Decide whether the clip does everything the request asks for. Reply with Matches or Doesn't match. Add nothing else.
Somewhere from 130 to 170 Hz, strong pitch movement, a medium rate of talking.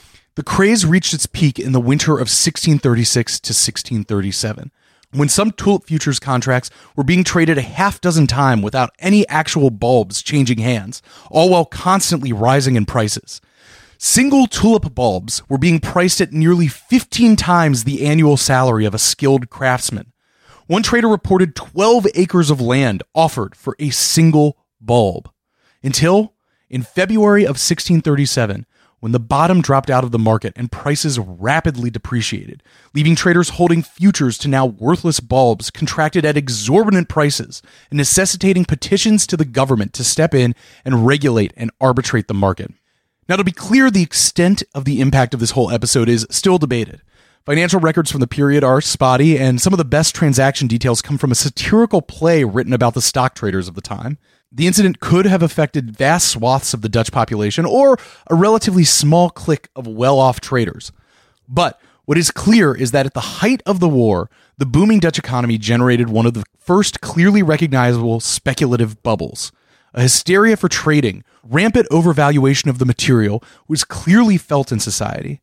Matches